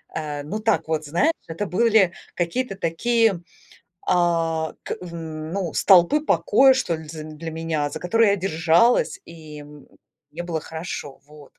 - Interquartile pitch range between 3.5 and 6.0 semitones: Yes, average, 4.1 semitones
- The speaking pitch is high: No, medium, 170 Hz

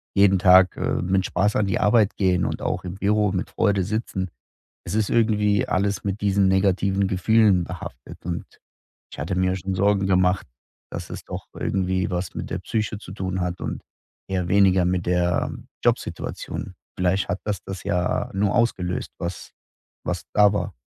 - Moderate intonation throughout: No, narrow, 1.9 semitones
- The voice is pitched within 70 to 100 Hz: Yes, very low, 95 Hz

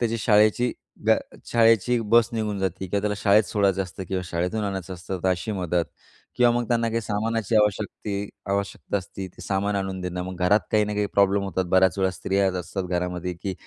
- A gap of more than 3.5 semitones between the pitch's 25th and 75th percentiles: No, narrow, 2.5 semitones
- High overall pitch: No, low, 100 Hz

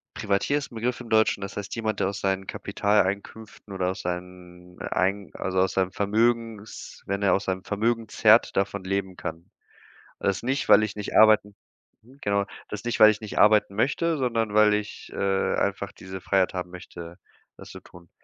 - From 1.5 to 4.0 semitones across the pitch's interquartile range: Yes, narrow, 2.5 semitones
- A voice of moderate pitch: No, low, 100 Hz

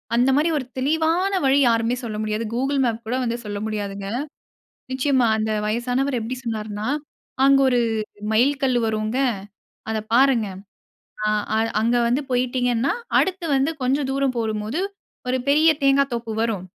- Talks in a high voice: Yes, high, 245 Hz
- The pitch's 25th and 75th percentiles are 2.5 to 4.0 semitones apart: Yes, average, 3.6 semitones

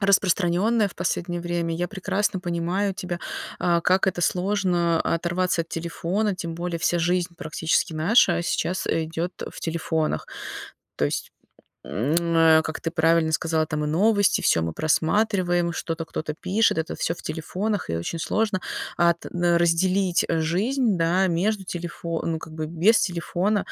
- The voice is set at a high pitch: No, medium, 175 Hz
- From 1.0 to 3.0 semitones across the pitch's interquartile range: Yes, narrow, 2.4 semitones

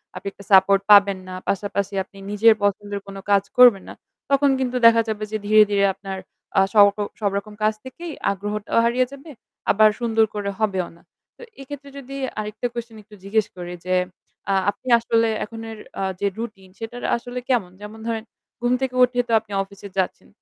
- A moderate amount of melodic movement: Yes, average, 3.0 semitones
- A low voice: No, high, 215 Hz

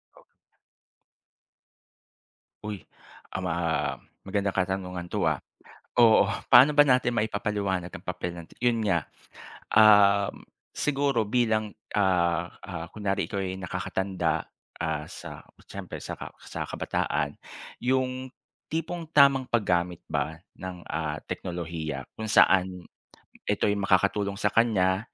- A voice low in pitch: Yes, low, 100 Hz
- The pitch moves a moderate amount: Yes, average, 4.0 semitones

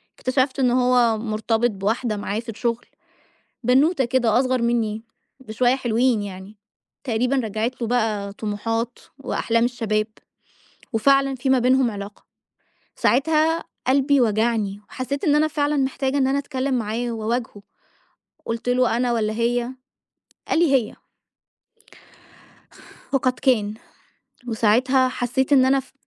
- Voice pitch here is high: Yes, high, 245 Hz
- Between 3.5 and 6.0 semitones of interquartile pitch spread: No, average, 3.0 semitones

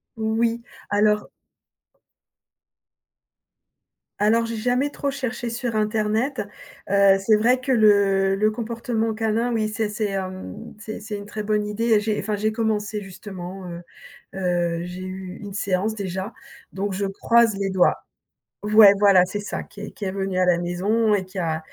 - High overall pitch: Yes, high, 210 Hz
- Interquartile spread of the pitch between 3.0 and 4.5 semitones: No, narrow, 2.5 semitones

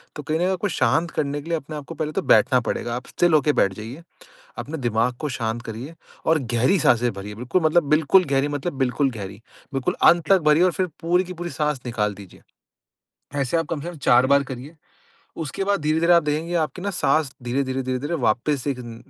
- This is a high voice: No, medium, 145 Hz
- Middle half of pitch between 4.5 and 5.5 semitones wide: Yes, average, 5.0 semitones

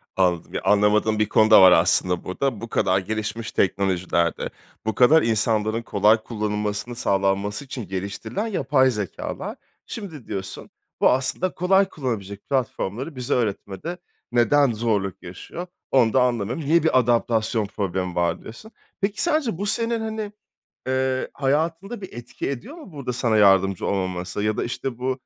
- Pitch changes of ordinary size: No, wide, 5.7 semitones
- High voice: No, low, 115 Hz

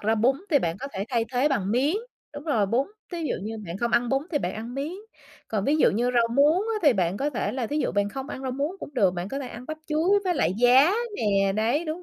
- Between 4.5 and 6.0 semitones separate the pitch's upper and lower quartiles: Yes, average, 5.3 semitones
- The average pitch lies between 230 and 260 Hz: Yes, very high, 250 Hz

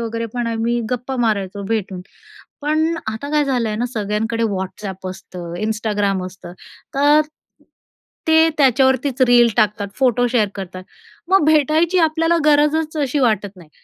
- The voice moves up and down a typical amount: No, wide, 6.0 semitones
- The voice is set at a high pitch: Yes, high, 235 Hz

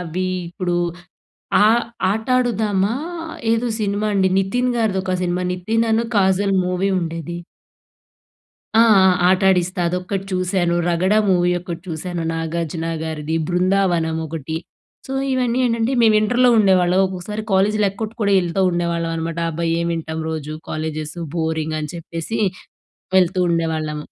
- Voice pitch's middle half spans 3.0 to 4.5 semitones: Yes, average, 3.4 semitones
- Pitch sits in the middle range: Yes, medium, 180 Hz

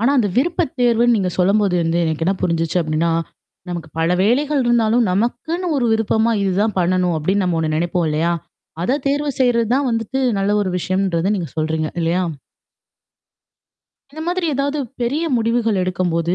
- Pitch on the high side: Yes, high, 200 Hz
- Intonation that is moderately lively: No, wide, 5.9 semitones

